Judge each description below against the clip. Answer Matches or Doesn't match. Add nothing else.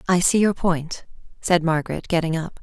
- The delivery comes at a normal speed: Matches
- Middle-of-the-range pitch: Matches